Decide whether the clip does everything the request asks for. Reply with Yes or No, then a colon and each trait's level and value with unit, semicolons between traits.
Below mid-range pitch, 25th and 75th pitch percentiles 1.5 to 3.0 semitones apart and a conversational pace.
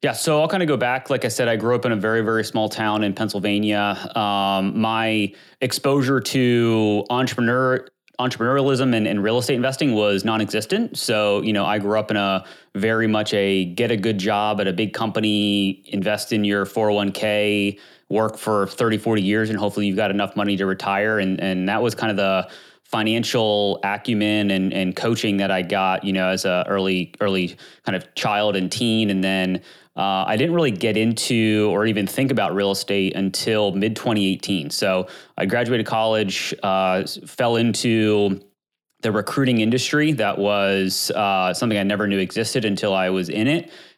Yes: low, 105 Hz; narrow, 2.5 semitones; average, 185 wpm